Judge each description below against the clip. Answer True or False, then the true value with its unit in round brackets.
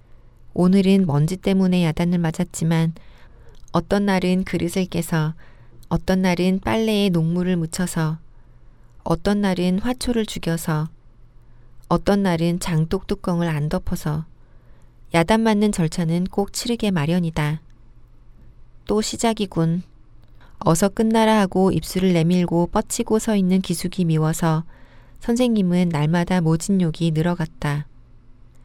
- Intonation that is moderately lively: True (4.0 semitones)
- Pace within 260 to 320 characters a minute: False (250 characters per minute)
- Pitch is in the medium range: True (170 Hz)